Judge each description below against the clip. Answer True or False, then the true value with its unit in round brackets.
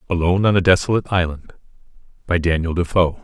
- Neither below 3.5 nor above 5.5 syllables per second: False (7.0 syllables/s)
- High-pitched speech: False (90 Hz)